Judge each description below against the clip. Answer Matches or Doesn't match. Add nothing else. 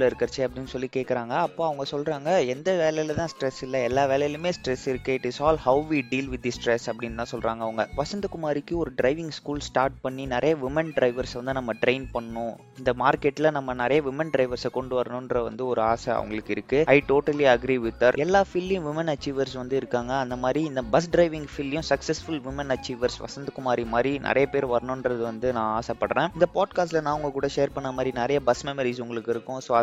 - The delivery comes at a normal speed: Doesn't match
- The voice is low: Matches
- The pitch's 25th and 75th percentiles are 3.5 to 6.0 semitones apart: Doesn't match